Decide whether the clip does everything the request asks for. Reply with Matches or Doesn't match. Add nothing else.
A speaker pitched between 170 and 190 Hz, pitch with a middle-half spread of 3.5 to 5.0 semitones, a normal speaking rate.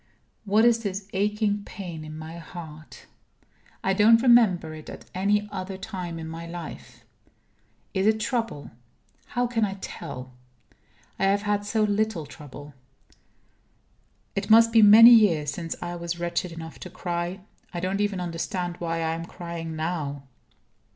Matches